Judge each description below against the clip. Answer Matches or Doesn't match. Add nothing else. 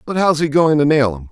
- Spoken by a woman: Doesn't match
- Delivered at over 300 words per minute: Matches